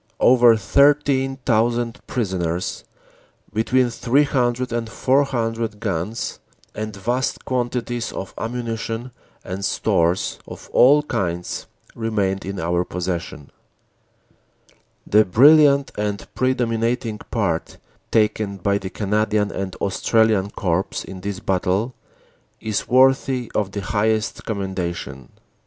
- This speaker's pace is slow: Yes, slow, 105 wpm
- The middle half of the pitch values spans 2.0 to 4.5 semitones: Yes, average, 4.0 semitones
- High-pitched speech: No, low, 110 Hz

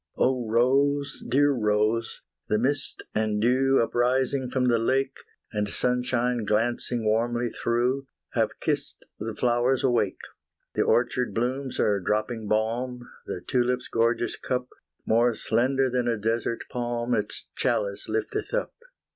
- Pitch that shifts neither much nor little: No, narrow, 2.3 semitones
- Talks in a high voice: No, low, 120 Hz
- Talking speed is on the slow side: Yes, slow, 130 wpm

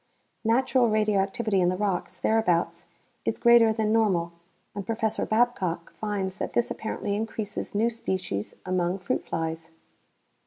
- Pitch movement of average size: Yes, average, 3.4 semitones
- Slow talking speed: Yes, slow, 130 wpm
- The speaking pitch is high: Yes, high, 210 Hz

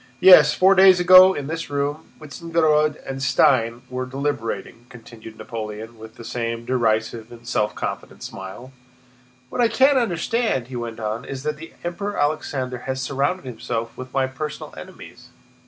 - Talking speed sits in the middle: Yes, average, 155 wpm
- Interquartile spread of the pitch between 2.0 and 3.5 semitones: No, average, 5.3 semitones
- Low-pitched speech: Yes, low, 130 Hz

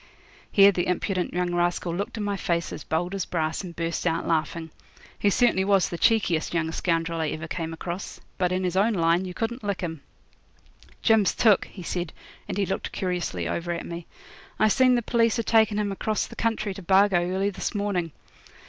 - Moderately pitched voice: Yes, medium, 180 Hz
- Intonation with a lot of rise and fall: No, average, 3.2 semitones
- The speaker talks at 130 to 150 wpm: No, average, 200 wpm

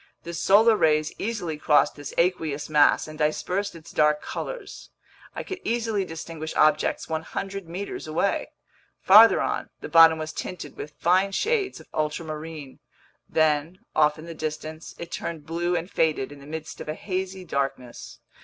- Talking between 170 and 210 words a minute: No, average, 160 wpm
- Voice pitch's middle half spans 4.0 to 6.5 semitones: No, average, 3.4 semitones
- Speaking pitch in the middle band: Yes, medium, 160 Hz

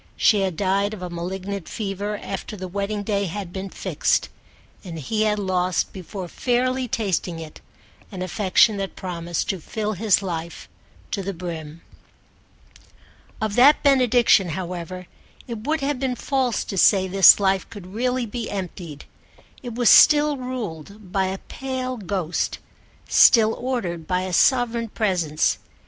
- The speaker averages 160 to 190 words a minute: No, average, 150 wpm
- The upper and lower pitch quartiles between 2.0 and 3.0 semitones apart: No, average, 4.1 semitones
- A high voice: Yes, high, 200 Hz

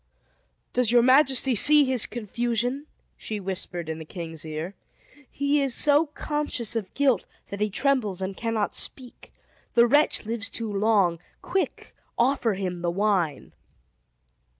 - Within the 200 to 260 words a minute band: No, average, 140 wpm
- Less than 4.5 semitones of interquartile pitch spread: No, wide, 5.6 semitones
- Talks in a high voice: Yes, high, 225 Hz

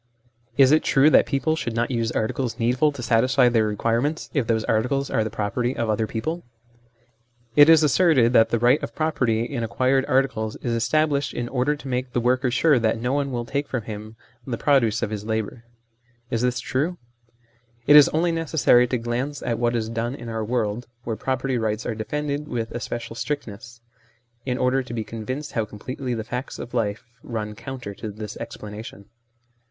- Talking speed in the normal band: Yes, average, 190 wpm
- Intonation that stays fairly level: No, average, 3.3 semitones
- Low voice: Yes, low, 120 Hz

